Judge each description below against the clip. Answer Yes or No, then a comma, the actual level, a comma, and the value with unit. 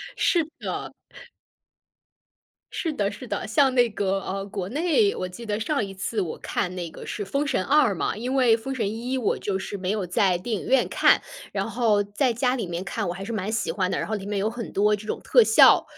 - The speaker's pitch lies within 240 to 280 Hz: No, high, 215 Hz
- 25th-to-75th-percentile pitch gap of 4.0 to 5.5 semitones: Yes, average, 4.3 semitones